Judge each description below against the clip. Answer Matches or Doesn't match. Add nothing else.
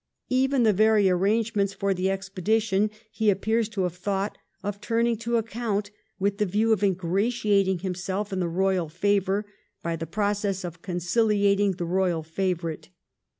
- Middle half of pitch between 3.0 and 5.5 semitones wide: Doesn't match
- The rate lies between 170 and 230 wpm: Doesn't match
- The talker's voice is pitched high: Matches